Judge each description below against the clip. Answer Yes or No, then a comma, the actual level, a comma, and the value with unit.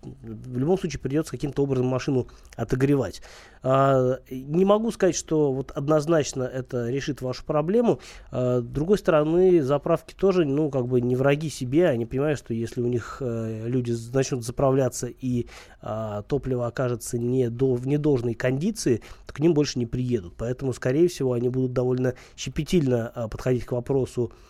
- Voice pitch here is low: Yes, low, 130 Hz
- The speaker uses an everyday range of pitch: Yes, average, 3.4 semitones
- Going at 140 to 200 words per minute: Yes, average, 145 wpm